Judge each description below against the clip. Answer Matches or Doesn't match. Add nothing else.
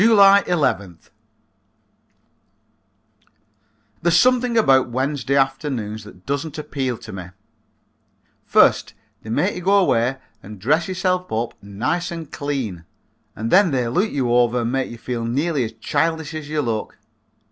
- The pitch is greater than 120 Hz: Matches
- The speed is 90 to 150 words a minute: Matches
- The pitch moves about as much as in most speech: Doesn't match